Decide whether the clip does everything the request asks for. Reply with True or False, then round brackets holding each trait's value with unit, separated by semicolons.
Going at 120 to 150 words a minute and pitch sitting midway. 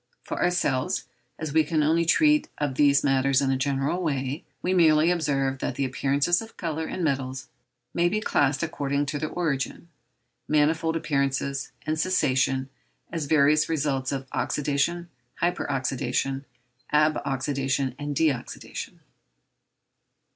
True (140 wpm; 145 Hz)